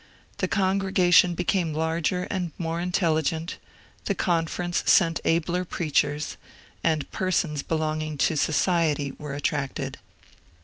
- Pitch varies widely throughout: No, narrow, 2.5 semitones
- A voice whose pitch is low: No, medium, 165 Hz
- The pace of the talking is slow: Yes, slow, 120 wpm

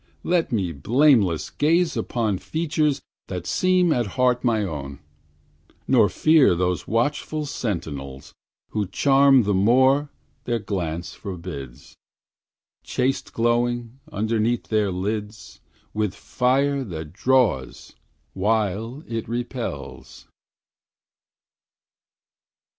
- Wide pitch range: Yes, wide, 6.2 semitones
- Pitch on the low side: Yes, low, 115 Hz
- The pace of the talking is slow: Yes, slow, 95 wpm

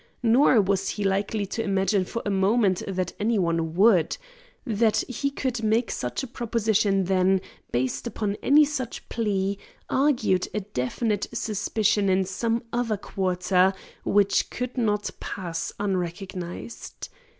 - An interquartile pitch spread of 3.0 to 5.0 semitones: Yes, average, 3.3 semitones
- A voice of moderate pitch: No, high, 205 Hz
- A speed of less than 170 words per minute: Yes, slow, 135 wpm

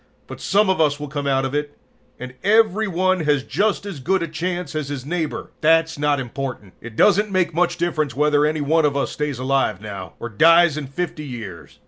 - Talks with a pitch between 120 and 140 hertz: No, medium, 150 Hz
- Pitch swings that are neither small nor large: Yes, average, 4.2 semitones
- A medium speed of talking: No, fast, 210 wpm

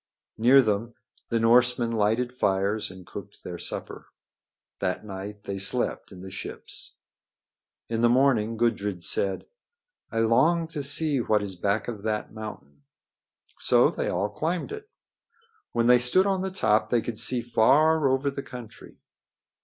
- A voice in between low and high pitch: No, low, 115 Hz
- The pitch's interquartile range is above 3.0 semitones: Yes, average, 4.1 semitones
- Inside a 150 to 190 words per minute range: Yes, average, 155 wpm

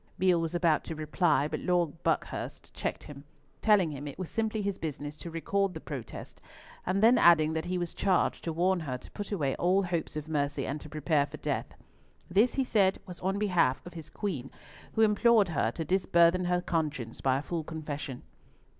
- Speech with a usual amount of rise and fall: Yes, average, 3.9 semitones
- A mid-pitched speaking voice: Yes, medium, 170 Hz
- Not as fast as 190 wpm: No, average, 200 wpm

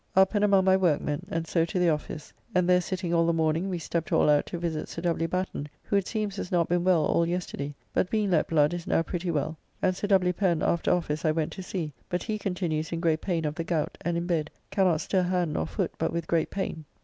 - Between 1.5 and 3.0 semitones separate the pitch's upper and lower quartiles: Yes, narrow, 2.5 semitones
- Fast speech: Yes, fast, 255 wpm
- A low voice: No, medium, 170 Hz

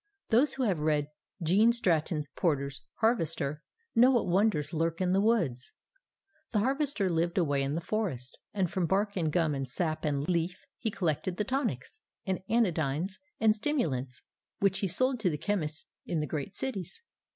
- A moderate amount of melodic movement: No, wide, 6.0 semitones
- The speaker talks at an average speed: Yes, average, 170 wpm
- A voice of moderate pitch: Yes, medium, 180 Hz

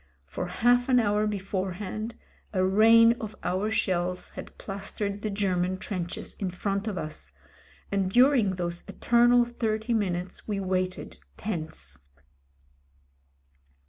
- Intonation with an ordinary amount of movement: Yes, average, 3.1 semitones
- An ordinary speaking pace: No, slow, 125 wpm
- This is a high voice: Yes, high, 200 Hz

